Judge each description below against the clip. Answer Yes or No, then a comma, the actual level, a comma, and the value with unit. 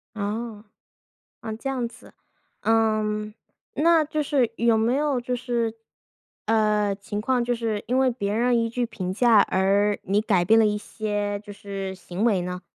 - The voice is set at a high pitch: Yes, high, 220 Hz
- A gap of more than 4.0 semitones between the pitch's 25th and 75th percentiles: No, average, 2.7 semitones